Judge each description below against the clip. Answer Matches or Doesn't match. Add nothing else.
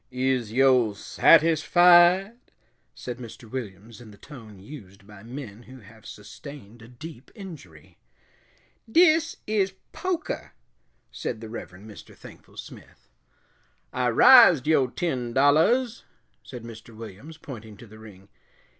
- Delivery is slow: Matches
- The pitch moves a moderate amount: Doesn't match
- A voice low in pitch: Matches